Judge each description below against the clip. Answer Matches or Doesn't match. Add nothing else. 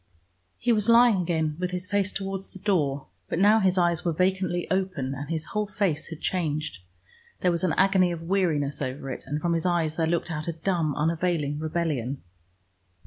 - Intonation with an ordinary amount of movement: Matches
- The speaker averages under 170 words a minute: Doesn't match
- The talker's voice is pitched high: Doesn't match